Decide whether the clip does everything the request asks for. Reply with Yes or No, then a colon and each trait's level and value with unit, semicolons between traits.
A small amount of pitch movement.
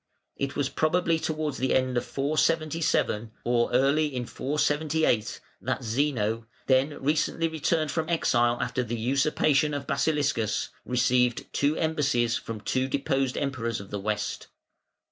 No: average, 4.2 semitones